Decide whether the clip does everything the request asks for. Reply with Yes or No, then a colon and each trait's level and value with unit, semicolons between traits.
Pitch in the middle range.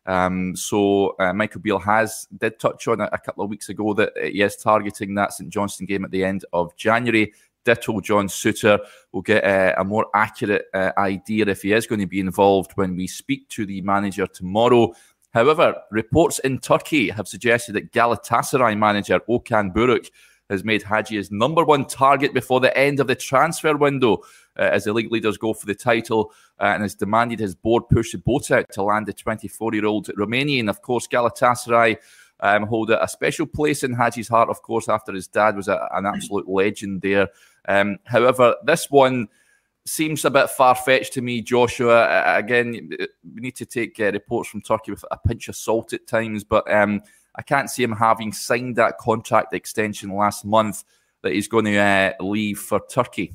No: low, 110 Hz